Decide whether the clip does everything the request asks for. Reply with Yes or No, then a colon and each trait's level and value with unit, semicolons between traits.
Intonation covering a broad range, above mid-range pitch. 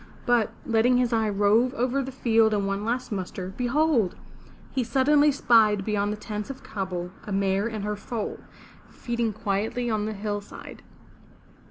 No: average, 3.2 semitones; high, 220 Hz